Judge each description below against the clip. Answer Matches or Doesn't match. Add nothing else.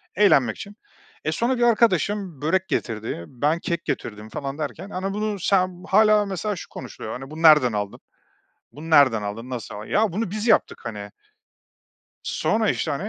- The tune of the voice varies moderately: Doesn't match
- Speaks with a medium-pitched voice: Matches